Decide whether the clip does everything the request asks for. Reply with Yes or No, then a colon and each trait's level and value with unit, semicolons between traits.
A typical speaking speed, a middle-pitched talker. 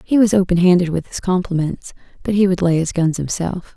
No: fast, 225 wpm; medium, 180 Hz